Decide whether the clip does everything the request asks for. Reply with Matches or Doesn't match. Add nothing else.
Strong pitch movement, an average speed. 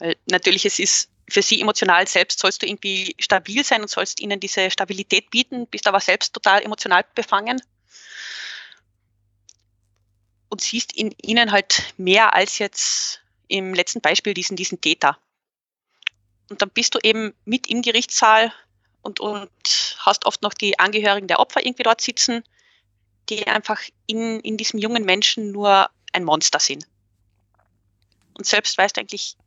Matches